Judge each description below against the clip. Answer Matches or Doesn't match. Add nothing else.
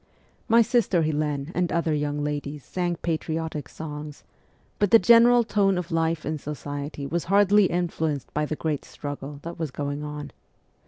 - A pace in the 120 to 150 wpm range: Doesn't match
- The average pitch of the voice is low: Doesn't match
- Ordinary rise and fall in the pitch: Matches